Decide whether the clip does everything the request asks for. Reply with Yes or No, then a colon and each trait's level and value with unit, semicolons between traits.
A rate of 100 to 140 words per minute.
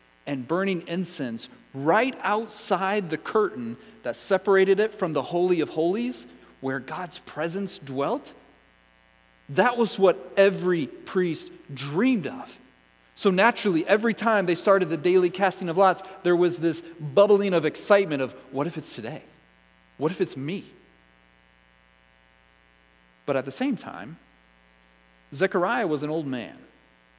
Yes: slow, 135 wpm